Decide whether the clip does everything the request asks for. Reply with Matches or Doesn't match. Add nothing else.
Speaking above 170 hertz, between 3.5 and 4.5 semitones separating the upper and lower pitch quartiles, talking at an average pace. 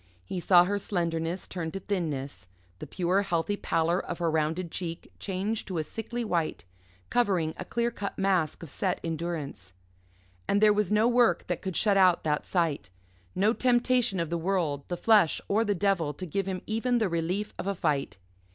Matches